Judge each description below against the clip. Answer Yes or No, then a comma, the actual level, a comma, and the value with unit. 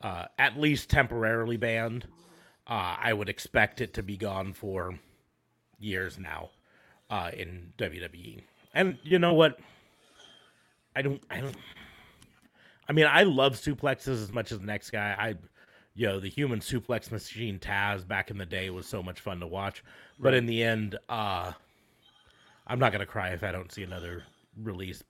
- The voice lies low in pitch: Yes, low, 110 Hz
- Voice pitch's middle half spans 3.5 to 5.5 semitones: Yes, average, 4.7 semitones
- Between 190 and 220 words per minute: No, average, 170 wpm